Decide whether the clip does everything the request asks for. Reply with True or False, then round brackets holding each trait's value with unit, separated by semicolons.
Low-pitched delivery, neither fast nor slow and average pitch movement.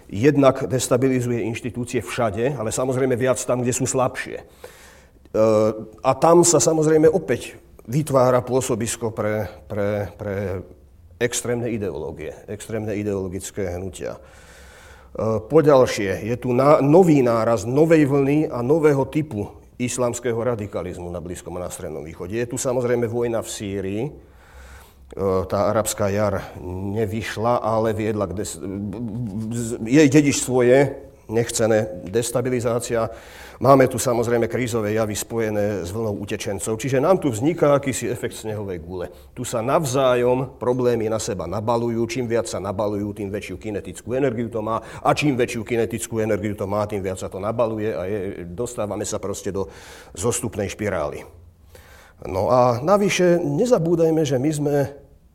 True (115 Hz; 140 wpm; 3.7 semitones)